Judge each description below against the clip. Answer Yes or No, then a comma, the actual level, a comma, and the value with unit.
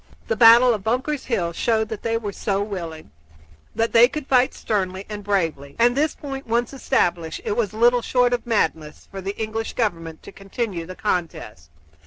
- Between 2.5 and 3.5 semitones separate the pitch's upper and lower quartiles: No, average, 4.7 semitones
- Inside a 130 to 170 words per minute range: No, average, 185 wpm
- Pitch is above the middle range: Yes, high, 215 Hz